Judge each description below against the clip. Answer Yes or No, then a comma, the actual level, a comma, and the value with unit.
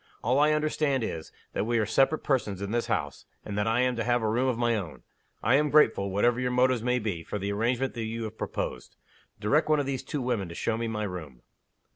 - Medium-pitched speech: No, low, 115 Hz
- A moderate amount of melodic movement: Yes, average, 3.7 semitones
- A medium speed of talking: No, fast, 245 wpm